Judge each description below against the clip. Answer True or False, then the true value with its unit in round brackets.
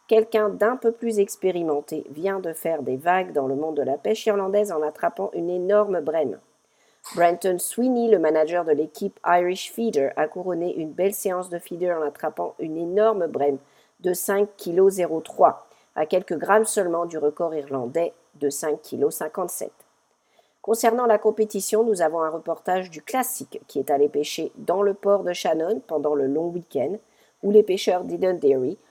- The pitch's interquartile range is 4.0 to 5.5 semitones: True (4.8 semitones)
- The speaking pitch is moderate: True (180 Hz)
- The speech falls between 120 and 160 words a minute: False (170 wpm)